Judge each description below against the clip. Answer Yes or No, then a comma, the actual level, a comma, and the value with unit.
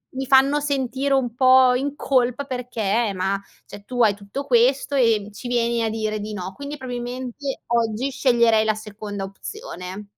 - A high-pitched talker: Yes, high, 240 Hz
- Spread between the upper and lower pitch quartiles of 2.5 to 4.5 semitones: Yes, average, 3.7 semitones